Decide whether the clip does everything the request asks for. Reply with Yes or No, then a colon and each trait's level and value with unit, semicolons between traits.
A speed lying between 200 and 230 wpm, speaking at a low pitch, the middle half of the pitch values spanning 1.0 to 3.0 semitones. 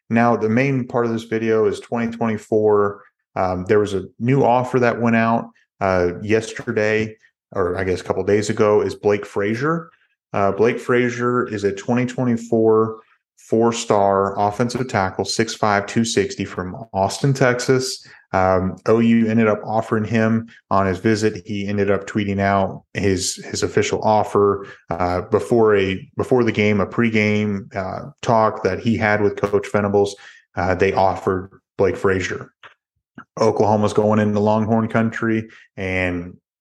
No: average, 150 wpm; low, 110 Hz; narrow, 2.4 semitones